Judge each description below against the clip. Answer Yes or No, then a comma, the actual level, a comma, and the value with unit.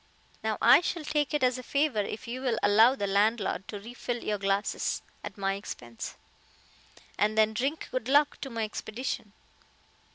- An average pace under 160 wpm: No, average, 170 wpm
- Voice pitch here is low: No, high, 225 Hz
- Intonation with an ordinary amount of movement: Yes, average, 4.1 semitones